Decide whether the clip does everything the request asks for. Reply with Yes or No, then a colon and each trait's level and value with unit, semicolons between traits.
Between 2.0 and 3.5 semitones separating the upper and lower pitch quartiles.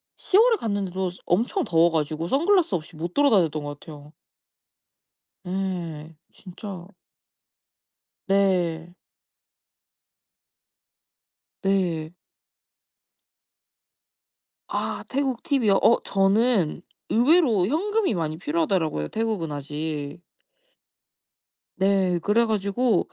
No: wide, 5.6 semitones